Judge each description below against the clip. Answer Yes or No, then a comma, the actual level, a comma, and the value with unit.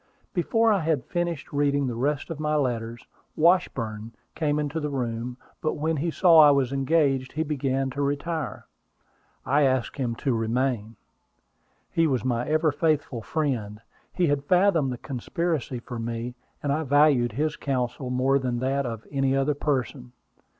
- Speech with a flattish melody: No, average, 3.6 semitones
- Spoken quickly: No, average, 165 wpm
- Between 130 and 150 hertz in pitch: Yes, medium, 140 Hz